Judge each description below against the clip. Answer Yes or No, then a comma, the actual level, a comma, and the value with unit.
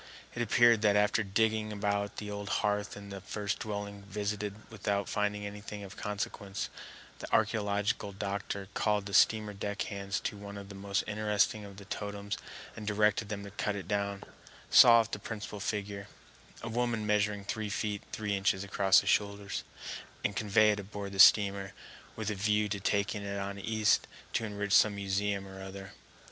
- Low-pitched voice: Yes, low, 100 Hz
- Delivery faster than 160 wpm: Yes, average, 175 wpm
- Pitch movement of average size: No, narrow, 1.0 semitones